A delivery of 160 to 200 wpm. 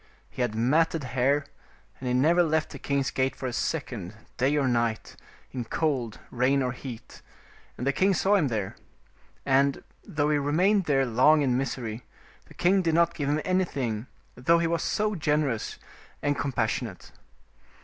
Yes: average, 170 wpm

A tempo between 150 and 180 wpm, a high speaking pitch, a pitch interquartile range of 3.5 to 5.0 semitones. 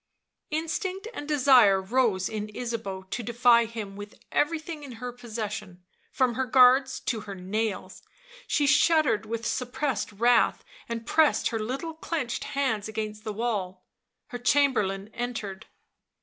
No: slow, 135 wpm; high, 235 Hz; average, 3.9 semitones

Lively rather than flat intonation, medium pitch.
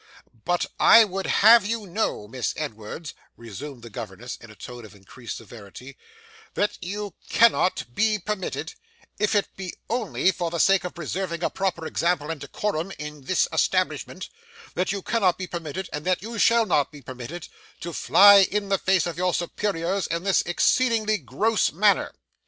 Yes: wide, 5.7 semitones; medium, 175 Hz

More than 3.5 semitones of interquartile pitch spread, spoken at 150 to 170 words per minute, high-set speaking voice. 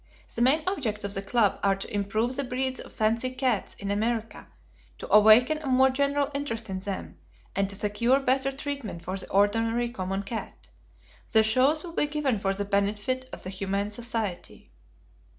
No: average, 4.6 semitones; average, 180 wpm; high, 225 Hz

